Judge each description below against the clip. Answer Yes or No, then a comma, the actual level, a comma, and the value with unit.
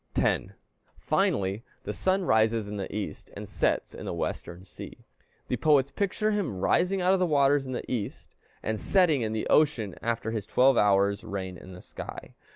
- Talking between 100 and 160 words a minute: No, average, 185 wpm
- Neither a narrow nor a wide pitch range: No, wide, 7.2 semitones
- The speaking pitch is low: Yes, low, 115 Hz